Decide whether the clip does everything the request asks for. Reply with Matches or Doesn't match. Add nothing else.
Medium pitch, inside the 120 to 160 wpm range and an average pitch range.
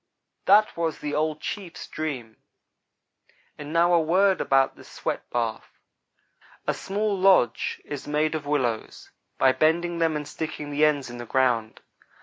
Matches